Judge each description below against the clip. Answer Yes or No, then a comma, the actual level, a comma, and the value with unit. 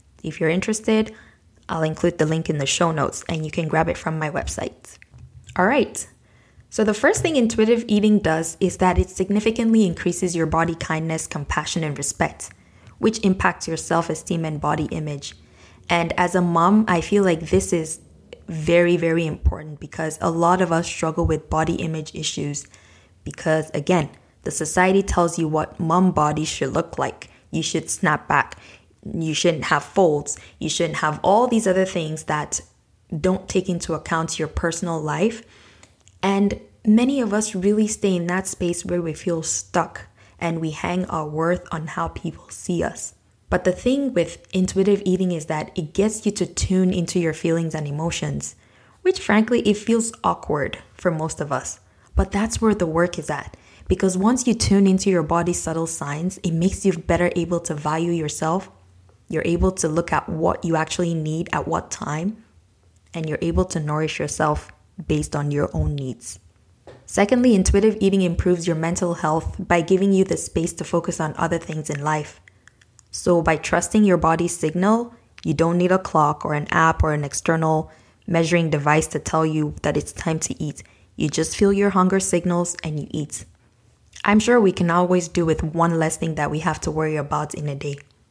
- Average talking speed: Yes, average, 185 wpm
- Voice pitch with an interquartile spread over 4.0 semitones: No, average, 3.2 semitones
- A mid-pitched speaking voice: Yes, medium, 165 Hz